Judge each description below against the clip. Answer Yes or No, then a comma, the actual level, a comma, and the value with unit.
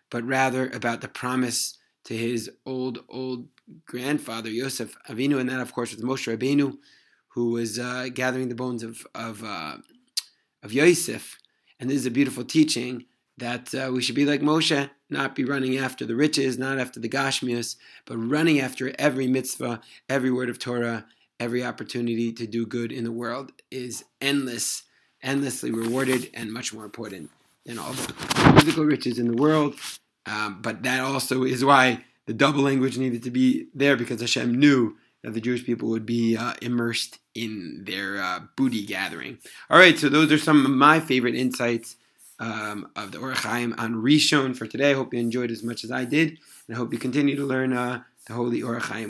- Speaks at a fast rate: No, average, 185 wpm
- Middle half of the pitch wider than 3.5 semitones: No, narrow, 2.5 semitones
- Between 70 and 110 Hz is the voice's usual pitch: No, low, 125 Hz